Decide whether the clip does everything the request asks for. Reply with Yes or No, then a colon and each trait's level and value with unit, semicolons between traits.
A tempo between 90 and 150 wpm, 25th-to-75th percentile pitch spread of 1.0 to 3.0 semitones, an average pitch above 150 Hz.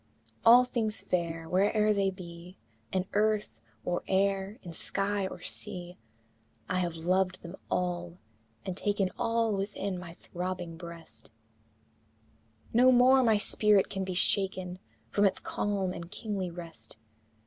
Yes: slow, 135 wpm; average, 2.7 semitones; high, 190 Hz